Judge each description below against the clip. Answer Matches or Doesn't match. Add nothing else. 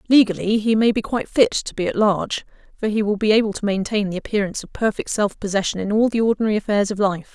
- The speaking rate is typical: Doesn't match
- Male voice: Doesn't match